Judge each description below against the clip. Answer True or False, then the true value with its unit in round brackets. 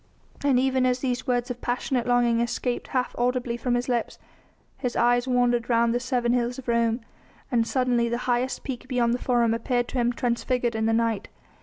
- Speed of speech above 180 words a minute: True (195 wpm)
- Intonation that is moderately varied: False (1.1 semitones)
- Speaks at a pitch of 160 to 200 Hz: False (245 Hz)